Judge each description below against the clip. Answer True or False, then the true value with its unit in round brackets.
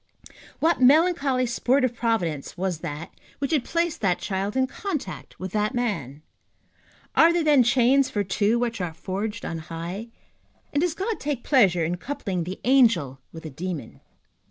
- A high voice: True (225 Hz)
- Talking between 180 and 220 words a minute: False (165 wpm)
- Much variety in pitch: True (7.4 semitones)